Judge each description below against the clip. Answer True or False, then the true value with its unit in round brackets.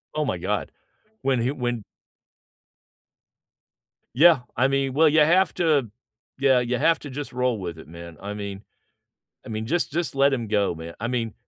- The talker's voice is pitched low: True (125 Hz)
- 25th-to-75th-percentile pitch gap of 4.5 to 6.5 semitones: True (5.2 semitones)